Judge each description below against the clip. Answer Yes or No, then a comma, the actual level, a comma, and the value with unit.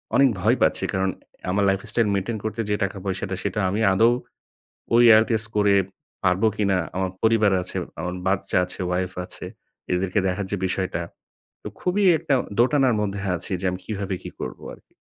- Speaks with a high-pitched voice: No, low, 100 Hz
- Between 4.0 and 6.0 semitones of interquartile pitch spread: No, average, 2.8 semitones